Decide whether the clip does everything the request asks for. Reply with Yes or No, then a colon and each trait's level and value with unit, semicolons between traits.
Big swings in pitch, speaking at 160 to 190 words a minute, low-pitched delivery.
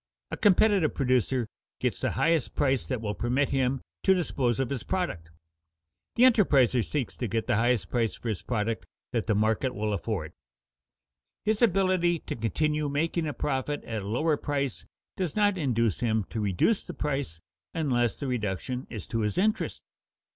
Yes: wide, 5.8 semitones; average, 170 wpm; low, 130 Hz